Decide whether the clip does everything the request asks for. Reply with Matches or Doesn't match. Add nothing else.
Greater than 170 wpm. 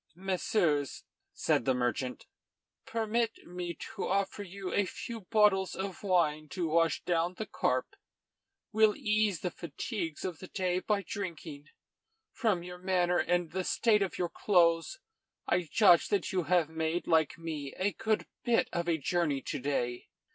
Doesn't match